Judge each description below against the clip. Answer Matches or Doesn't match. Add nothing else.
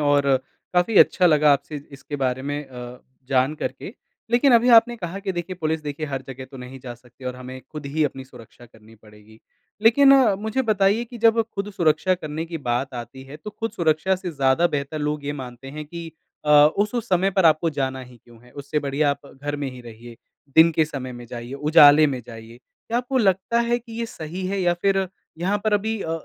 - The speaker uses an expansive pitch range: Matches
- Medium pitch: Matches